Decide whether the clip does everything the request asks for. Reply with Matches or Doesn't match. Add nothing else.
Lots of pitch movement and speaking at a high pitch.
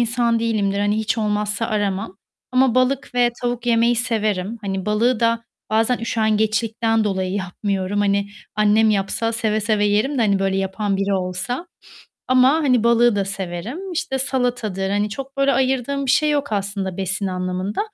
Doesn't match